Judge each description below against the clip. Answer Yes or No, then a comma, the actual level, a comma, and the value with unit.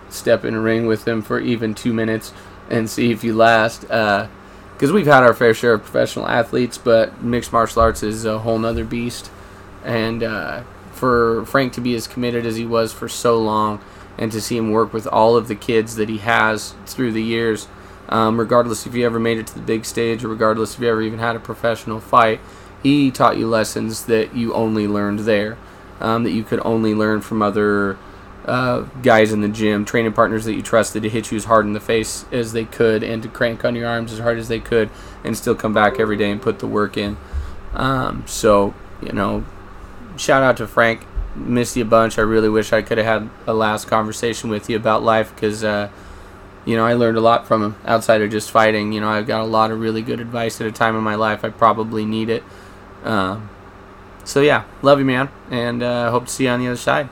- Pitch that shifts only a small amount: Yes, narrow, 1.7 semitones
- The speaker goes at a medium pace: No, fast, 230 wpm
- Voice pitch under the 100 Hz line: No, low, 110 Hz